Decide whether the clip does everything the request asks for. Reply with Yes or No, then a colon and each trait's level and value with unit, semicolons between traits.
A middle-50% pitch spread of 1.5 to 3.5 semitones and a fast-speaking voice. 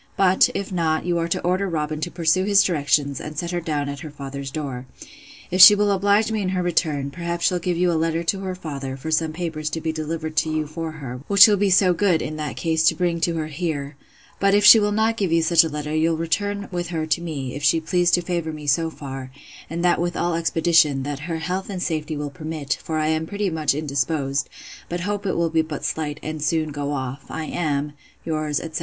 Yes: average, 2.8 semitones; fast, 245 wpm